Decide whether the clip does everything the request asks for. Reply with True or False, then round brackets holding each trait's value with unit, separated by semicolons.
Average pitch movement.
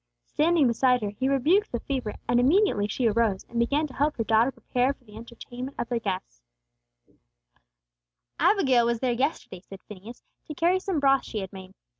True (4.1 semitones)